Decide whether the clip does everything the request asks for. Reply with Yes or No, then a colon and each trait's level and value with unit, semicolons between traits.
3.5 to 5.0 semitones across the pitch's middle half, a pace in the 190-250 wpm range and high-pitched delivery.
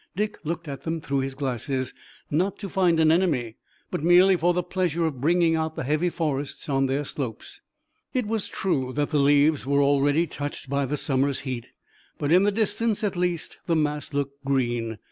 No: average, 4.1 semitones; average, 195 wpm; medium, 150 Hz